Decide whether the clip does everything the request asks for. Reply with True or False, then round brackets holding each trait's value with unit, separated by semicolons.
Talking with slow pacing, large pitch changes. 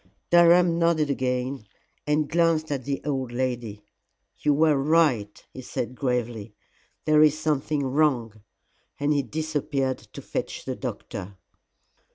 False (130 wpm; 3.7 semitones)